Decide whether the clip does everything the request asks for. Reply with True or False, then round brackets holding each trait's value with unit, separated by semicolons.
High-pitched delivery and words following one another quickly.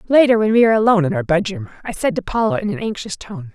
True (220 Hz; 270 wpm)